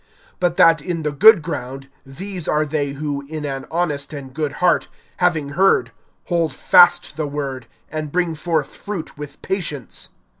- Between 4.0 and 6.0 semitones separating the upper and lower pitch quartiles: No, average, 3.6 semitones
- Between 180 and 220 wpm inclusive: No, average, 160 wpm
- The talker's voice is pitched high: No, medium, 155 Hz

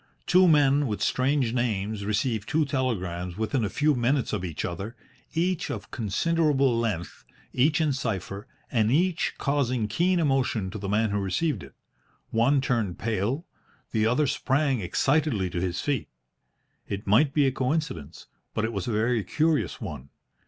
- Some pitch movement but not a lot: No, wide, 5.9 semitones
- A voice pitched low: Yes, low, 120 Hz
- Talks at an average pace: Yes, average, 160 wpm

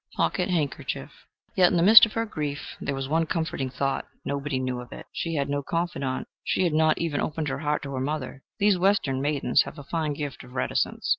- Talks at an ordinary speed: No, fast, 220 wpm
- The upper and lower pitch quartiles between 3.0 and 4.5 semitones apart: Yes, average, 3.5 semitones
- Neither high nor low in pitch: Yes, medium, 150 Hz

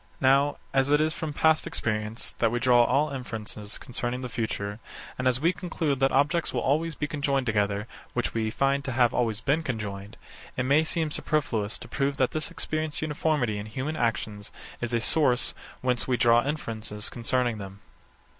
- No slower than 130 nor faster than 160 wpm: No, average, 185 wpm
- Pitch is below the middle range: Yes, low, 125 Hz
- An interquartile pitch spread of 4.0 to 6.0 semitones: Yes, average, 4.6 semitones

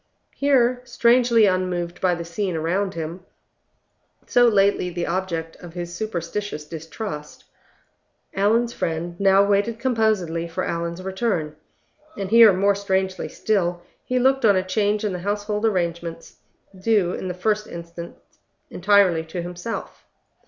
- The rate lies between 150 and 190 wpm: No, slow, 135 wpm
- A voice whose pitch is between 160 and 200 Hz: Yes, high, 190 Hz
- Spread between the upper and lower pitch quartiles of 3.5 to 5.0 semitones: Yes, average, 3.8 semitones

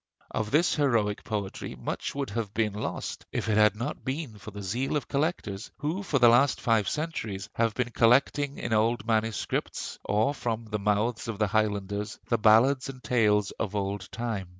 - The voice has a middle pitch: No, low, 110 Hz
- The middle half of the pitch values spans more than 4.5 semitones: No, average, 3.8 semitones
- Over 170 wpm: Yes, average, 185 wpm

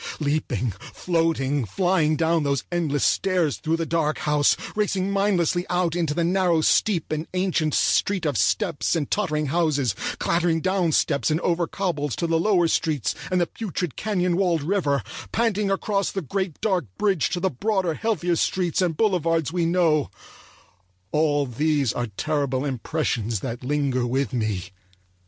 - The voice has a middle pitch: Yes, medium, 165 Hz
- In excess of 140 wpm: Yes, average, 155 wpm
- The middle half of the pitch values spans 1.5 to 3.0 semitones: No, average, 4.0 semitones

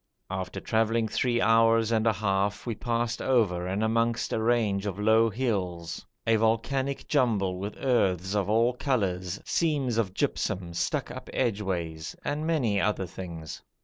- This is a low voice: Yes, low, 110 Hz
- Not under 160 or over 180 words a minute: No, average, 150 wpm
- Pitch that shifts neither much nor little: Yes, average, 3.7 semitones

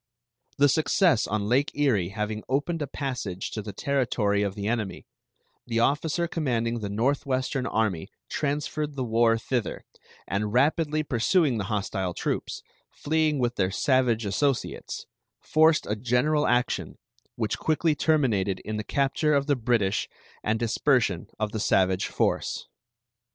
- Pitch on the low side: Yes, low, 120 Hz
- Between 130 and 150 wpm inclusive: Yes, average, 140 wpm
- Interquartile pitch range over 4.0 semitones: Yes, average, 5.3 semitones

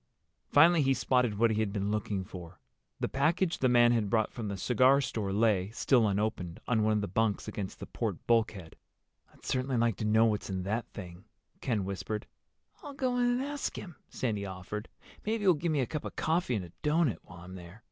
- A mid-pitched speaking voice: No, low, 110 Hz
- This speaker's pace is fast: Yes, fast, 215 wpm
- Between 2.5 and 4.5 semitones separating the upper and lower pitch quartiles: No, average, 5.3 semitones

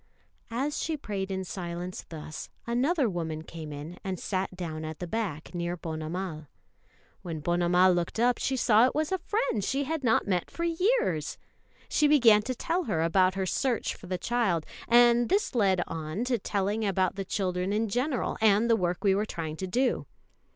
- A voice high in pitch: Yes, high, 195 Hz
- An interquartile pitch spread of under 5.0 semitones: No, wide, 5.6 semitones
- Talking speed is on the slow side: No, average, 190 wpm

